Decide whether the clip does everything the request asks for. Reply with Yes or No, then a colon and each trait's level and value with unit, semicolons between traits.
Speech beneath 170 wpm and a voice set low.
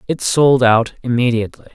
Yes: average, 140 wpm; low, 120 Hz